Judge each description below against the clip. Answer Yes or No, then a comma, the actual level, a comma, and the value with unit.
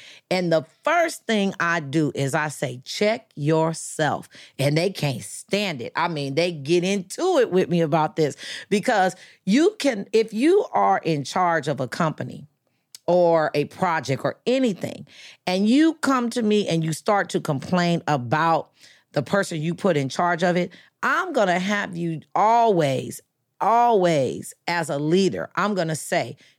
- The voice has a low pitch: No, medium, 175 Hz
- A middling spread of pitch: Yes, average, 4.5 semitones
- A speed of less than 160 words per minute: No, average, 165 wpm